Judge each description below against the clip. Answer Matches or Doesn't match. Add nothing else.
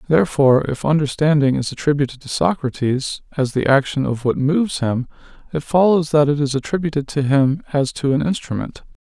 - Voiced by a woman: Doesn't match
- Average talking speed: Matches